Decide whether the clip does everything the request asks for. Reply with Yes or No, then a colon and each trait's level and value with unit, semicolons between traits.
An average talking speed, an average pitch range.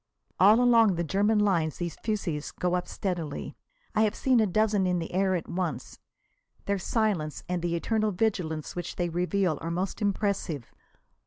Yes: average, 170 wpm; average, 3.5 semitones